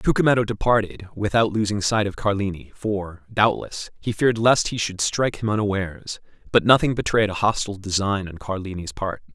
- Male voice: Yes, male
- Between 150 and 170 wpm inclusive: Yes, average, 165 wpm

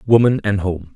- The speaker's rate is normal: Yes, average, 190 wpm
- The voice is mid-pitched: No, low, 100 Hz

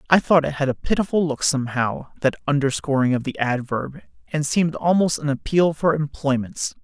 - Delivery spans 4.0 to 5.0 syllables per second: No, 5.5 syllables/s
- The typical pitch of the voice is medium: Yes, medium, 145 Hz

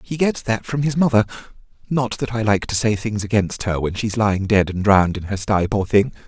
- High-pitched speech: No, low, 110 Hz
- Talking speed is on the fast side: Yes, fast, 240 wpm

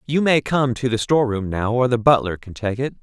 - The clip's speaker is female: No, male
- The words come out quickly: Yes, fast, 275 wpm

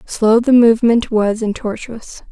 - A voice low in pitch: No, high, 225 Hz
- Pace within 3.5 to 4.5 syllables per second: Yes, 4.2 syllables/s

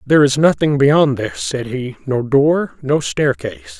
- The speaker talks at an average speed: Yes, average, 175 wpm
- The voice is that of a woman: No, male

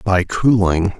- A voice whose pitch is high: No, low, 100 Hz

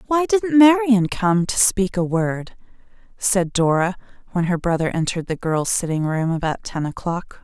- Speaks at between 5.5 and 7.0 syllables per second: No, 4.6 syllables/s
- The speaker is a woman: Yes, female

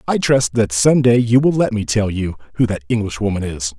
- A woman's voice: No, male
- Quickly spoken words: Yes, fast, 240 wpm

